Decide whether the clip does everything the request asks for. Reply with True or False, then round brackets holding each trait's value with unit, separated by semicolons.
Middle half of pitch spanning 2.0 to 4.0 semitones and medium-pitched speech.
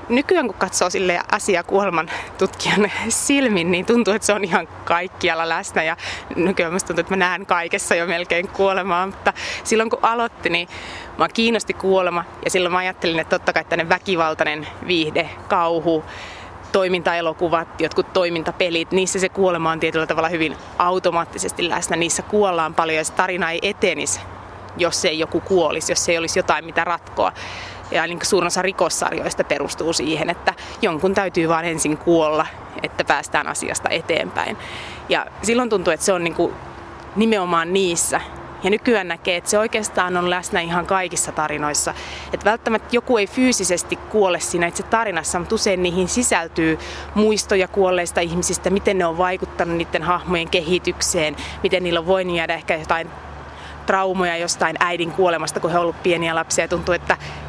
True (2.5 semitones; 175 Hz)